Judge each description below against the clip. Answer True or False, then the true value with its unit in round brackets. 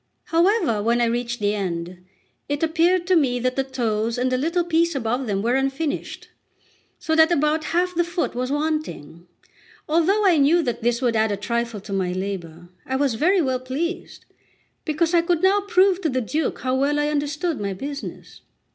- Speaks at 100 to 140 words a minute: False (185 wpm)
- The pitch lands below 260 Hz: False (275 Hz)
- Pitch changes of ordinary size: False (6.2 semitones)